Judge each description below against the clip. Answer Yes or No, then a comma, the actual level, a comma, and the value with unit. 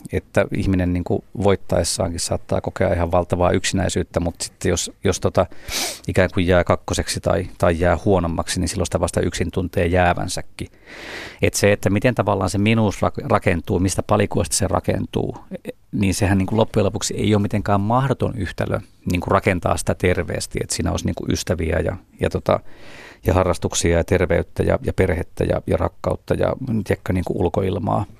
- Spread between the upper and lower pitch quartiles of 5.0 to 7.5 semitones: No, narrow, 2.6 semitones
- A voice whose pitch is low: Yes, very low, 95 Hz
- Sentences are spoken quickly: Yes, fast, 165 wpm